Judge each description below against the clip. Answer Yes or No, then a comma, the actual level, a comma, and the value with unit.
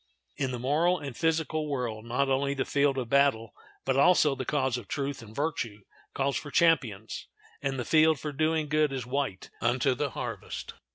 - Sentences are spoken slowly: No, average, 185 wpm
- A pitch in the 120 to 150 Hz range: Yes, medium, 140 Hz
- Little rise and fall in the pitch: No, average, 3.2 semitones